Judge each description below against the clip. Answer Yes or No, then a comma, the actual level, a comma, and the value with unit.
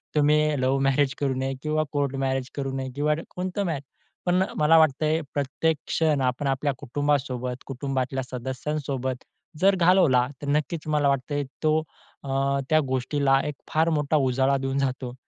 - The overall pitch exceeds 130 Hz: Yes, medium, 140 Hz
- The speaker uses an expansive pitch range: No, narrow, 2.4 semitones